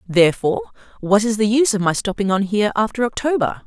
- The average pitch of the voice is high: Yes, high, 215 Hz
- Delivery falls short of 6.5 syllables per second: No, 6.7 syllables/s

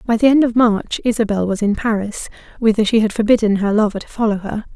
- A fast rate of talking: Yes, fast, 225 wpm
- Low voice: No, high, 220 Hz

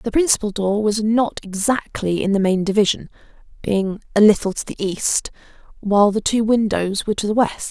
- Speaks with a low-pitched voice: No, high, 205 Hz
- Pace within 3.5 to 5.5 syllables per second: Yes, 5.2 syllables/s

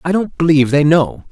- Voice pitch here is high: No, medium, 155 Hz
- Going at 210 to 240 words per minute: Yes, fast, 225 wpm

